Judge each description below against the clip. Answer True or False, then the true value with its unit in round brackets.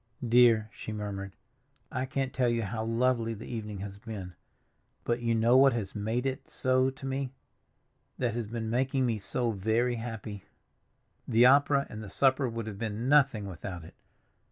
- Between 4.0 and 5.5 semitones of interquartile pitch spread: False (3.2 semitones)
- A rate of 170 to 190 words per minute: True (175 wpm)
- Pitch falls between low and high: False (115 Hz)